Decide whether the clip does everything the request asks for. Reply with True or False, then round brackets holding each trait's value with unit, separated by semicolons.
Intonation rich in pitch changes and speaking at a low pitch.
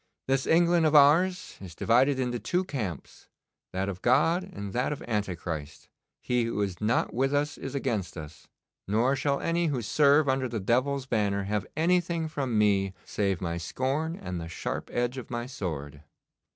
True (6.6 semitones; 125 Hz)